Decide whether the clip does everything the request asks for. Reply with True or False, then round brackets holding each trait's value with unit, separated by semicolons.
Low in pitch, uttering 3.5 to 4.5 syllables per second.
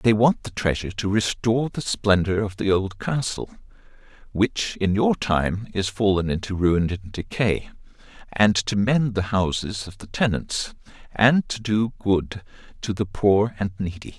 True (105 Hz; 4.3 syllables/s)